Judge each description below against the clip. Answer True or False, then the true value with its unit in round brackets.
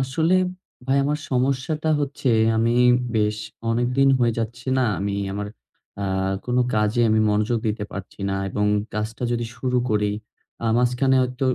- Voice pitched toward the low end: True (120 Hz)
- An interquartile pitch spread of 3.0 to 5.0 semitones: True (3.6 semitones)